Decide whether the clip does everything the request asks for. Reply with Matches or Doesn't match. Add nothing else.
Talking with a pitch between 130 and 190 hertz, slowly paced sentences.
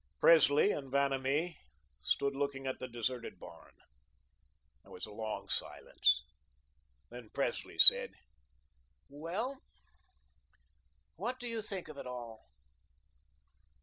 Matches